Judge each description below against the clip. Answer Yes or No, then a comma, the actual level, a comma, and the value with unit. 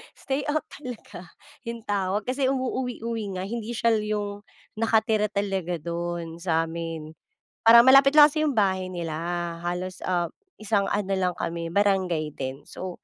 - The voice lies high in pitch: Yes, high, 200 Hz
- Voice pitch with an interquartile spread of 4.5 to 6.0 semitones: Yes, average, 5.1 semitones